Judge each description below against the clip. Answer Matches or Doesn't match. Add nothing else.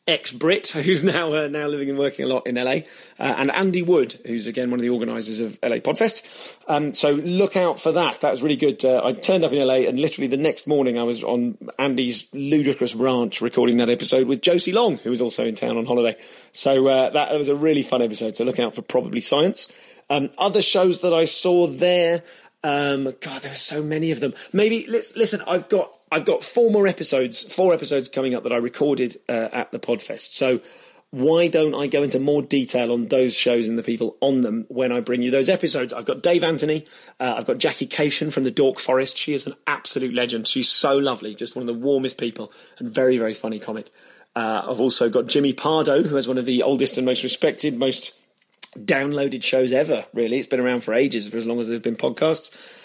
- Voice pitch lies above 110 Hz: Matches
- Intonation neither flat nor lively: Matches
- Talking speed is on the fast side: Matches